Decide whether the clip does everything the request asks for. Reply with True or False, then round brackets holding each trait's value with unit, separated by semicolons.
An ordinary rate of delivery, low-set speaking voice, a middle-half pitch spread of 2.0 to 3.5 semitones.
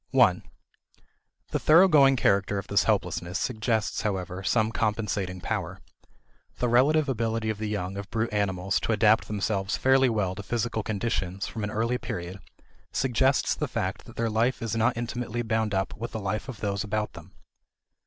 True (170 wpm; 110 Hz; 2.9 semitones)